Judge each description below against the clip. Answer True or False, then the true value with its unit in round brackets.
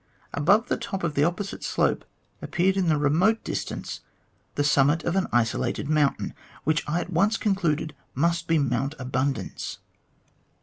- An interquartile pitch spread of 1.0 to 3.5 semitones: False (4.7 semitones)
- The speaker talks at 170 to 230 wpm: False (155 wpm)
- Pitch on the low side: False (160 Hz)